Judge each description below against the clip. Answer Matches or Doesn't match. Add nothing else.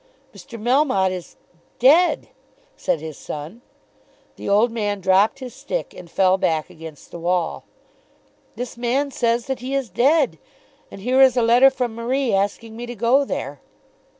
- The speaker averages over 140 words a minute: Matches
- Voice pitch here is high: Matches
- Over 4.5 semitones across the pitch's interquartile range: Matches